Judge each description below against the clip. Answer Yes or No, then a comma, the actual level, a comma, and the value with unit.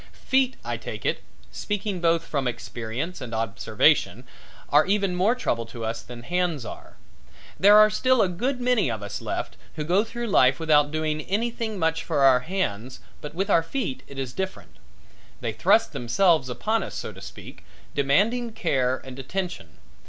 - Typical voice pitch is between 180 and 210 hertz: No, medium, 165 Hz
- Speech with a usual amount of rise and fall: No, wide, 7.9 semitones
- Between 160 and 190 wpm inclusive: Yes, average, 175 wpm